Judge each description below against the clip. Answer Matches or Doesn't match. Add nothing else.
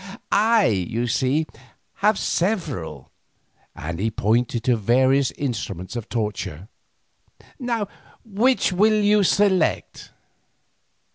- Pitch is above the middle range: Doesn't match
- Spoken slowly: Matches